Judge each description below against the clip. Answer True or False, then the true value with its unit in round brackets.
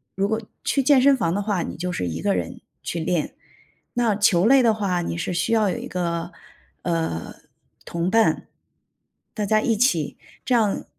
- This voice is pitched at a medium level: False (195 Hz)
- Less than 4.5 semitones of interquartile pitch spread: False (4.8 semitones)